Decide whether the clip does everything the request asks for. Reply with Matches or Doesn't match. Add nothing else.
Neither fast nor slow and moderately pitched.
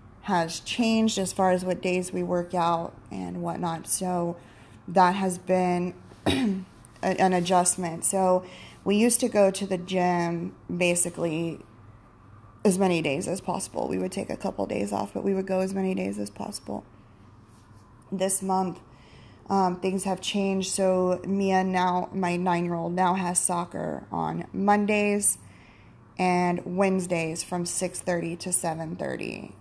Matches